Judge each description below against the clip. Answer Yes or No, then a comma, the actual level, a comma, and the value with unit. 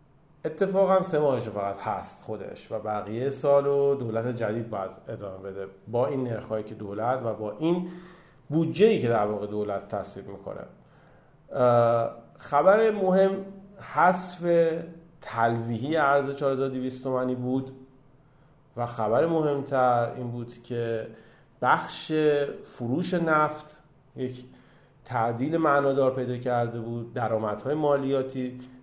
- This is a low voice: Yes, low, 130 Hz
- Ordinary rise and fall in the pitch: Yes, average, 4.6 semitones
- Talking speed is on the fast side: No, average, 115 wpm